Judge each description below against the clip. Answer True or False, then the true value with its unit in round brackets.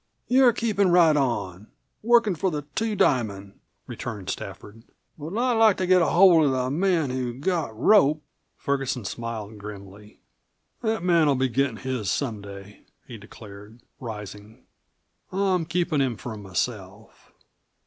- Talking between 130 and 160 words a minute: True (140 wpm)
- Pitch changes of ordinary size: False (8.9 semitones)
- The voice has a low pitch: True (130 Hz)